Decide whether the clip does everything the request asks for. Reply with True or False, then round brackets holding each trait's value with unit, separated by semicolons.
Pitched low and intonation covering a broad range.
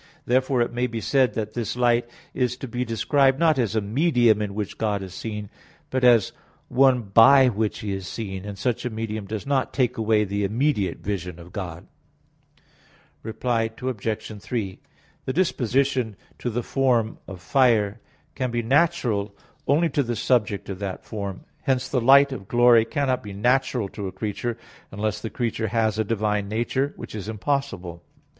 False (115 Hz; 3.7 semitones)